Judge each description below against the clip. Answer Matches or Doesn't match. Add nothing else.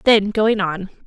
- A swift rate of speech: Doesn't match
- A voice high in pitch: Matches